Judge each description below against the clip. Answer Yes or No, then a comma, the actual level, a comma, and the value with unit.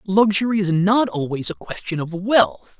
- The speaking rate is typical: Yes, average, 170 wpm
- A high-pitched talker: Yes, high, 195 Hz